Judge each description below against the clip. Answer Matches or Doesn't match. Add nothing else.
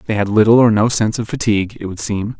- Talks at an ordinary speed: Doesn't match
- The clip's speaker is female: Doesn't match